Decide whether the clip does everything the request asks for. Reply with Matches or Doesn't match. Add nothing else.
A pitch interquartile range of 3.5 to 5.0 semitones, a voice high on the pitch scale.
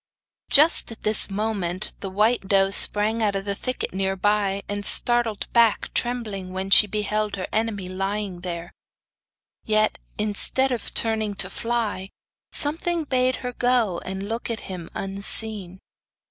Doesn't match